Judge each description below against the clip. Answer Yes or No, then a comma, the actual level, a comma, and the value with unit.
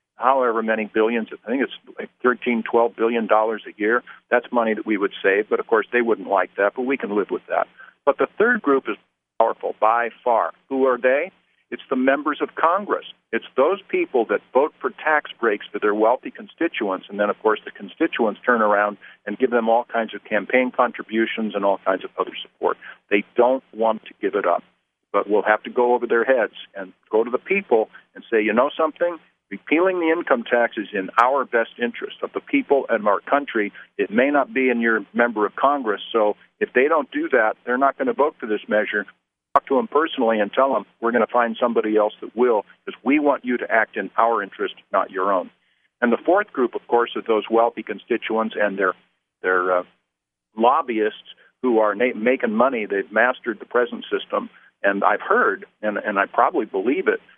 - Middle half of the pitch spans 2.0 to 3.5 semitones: No, average, 5.3 semitones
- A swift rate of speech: Yes, fast, 215 wpm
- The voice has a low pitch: Yes, low, 120 Hz